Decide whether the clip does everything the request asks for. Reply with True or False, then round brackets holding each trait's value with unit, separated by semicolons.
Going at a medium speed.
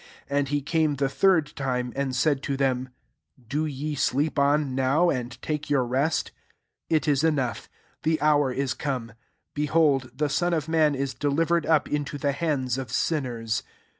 True (175 wpm)